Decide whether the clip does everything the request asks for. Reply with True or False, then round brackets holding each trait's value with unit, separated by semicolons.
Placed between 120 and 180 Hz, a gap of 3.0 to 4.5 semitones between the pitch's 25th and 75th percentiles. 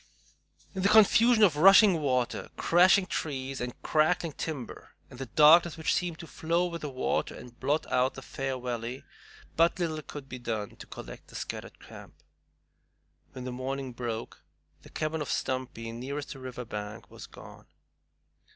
False (140 Hz; 4.9 semitones)